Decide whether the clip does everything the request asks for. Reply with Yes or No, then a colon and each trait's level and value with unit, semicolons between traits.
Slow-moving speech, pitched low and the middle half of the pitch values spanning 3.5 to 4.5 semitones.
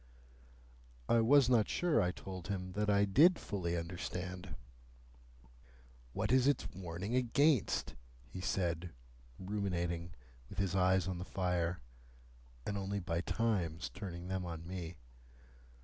No: slow, 130 wpm; very low, 95 Hz; average, 2.9 semitones